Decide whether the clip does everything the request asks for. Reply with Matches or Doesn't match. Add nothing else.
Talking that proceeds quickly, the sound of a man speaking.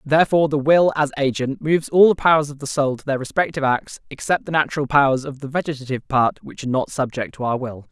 Matches